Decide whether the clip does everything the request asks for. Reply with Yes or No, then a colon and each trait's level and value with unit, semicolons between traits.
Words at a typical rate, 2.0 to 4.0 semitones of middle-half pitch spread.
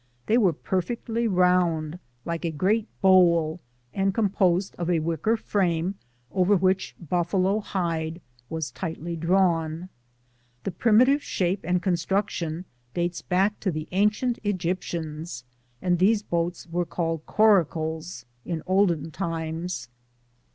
No: slow, 120 wpm; average, 2.8 semitones